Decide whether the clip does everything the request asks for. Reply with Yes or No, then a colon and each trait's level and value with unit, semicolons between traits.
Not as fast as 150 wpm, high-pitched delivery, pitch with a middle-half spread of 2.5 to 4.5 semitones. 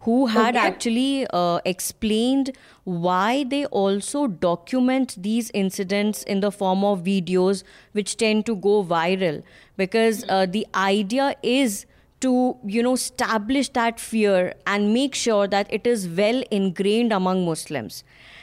Yes: slow, 135 wpm; high, 210 Hz; average, 3.9 semitones